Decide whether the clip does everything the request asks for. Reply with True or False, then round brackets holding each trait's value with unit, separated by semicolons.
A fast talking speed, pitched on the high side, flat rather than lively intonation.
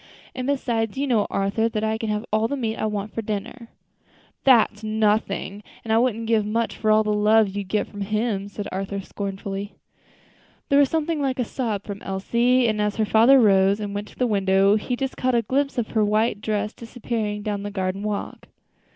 True (210 wpm; 215 Hz; 2.3 semitones)